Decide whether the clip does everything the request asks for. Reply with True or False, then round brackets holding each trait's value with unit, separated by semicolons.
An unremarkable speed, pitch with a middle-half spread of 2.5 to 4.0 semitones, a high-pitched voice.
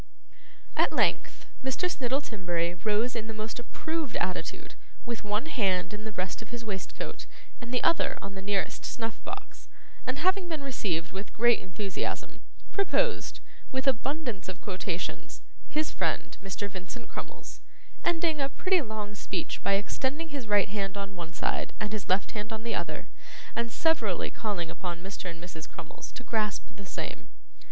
False (165 wpm; 5.2 semitones; 215 Hz)